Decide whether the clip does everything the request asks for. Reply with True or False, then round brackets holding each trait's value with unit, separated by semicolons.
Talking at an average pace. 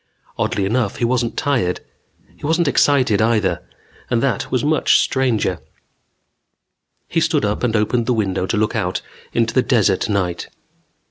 True (150 wpm)